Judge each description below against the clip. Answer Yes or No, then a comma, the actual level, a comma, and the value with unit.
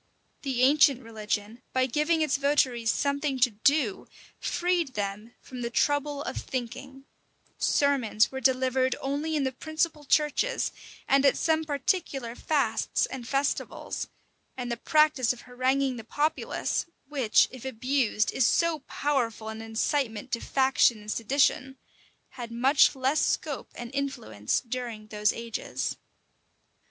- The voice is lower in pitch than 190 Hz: No, very high, 265 Hz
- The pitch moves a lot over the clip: No, average, 3.5 semitones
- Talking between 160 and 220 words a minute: No, slow, 135 wpm